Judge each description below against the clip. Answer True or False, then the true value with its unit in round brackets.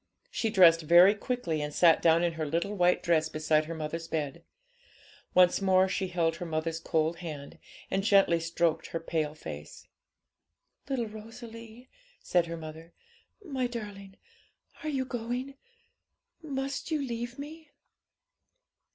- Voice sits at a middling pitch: True (180 Hz)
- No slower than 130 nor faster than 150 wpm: True (140 wpm)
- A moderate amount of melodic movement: False (6.0 semitones)